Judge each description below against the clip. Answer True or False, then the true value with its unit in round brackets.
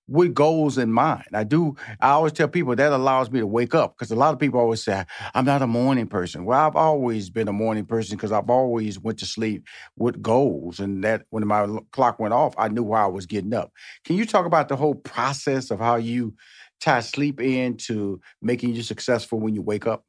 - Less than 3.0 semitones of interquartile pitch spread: False (3.8 semitones)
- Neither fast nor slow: False (235 wpm)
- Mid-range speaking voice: False (120 Hz)